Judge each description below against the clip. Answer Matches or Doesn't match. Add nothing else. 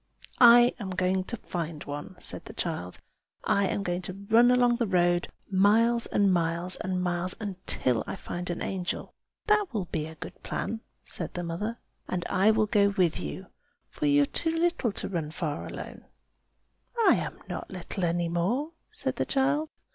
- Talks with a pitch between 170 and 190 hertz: Matches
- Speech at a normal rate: Matches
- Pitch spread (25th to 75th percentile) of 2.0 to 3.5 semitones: Doesn't match